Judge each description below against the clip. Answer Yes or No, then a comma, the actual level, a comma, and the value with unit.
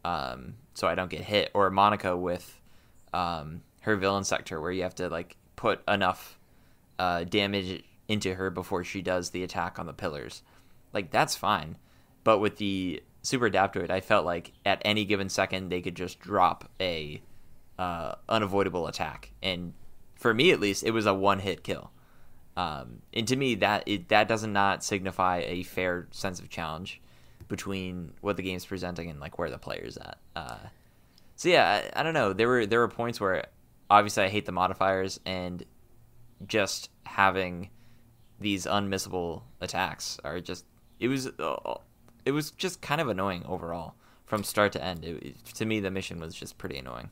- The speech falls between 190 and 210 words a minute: No, average, 180 wpm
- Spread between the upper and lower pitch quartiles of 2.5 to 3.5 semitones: Yes, average, 2.8 semitones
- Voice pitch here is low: Yes, very low, 95 Hz